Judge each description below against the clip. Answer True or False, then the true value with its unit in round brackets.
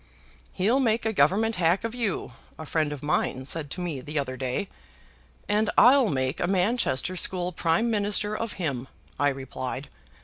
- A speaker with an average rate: True (170 wpm)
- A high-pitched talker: False (180 Hz)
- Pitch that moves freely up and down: True (7.1 semitones)